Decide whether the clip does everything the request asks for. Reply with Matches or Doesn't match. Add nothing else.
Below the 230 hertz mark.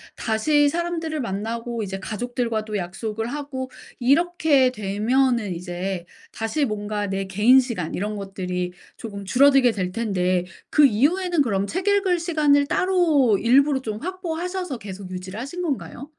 Doesn't match